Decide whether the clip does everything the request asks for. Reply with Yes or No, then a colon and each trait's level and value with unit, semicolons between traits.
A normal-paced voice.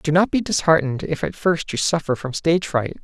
No: fast, 235 wpm